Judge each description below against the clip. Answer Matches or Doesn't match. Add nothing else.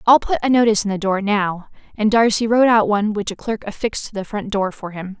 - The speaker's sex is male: Doesn't match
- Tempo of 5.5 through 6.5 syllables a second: Matches